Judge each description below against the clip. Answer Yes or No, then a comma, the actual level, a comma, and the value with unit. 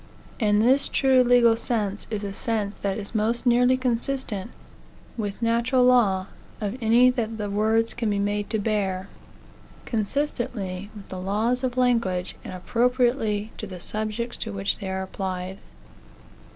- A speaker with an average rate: Yes, average, 150 wpm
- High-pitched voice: Yes, high, 220 Hz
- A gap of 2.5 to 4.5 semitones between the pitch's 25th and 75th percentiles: Yes, average, 3.2 semitones